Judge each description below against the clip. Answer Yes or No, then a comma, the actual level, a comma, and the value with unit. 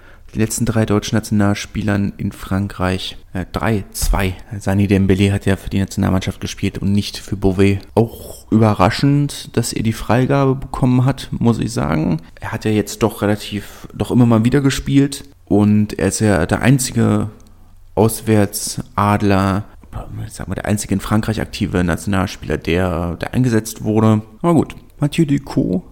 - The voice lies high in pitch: No, low, 105 Hz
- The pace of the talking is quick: No, average, 155 wpm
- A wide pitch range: No, narrow, 2.6 semitones